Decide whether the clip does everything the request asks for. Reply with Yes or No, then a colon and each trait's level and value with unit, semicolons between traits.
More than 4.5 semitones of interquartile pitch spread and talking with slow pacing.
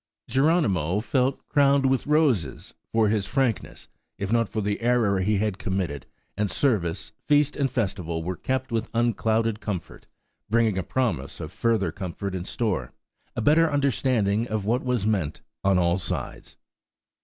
No: average, 5.0 semitones; average, 150 wpm